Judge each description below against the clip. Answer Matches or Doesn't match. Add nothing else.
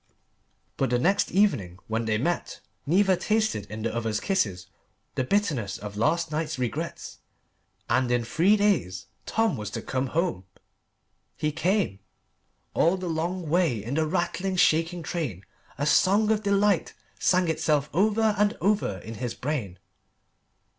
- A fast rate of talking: Doesn't match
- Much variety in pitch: Matches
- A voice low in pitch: Doesn't match